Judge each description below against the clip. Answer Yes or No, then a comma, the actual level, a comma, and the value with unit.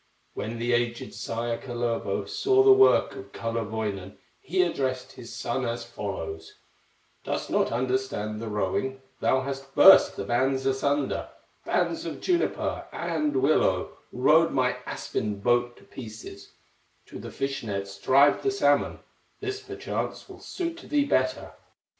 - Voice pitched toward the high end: No, low, 130 Hz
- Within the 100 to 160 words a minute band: Yes, average, 140 wpm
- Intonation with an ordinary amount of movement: Yes, average, 4.2 semitones